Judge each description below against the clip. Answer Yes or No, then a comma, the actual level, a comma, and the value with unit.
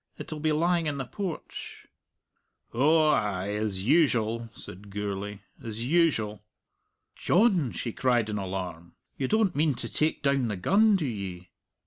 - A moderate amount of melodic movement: No, wide, 7.3 semitones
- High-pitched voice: No, low, 120 Hz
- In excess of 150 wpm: No, average, 145 wpm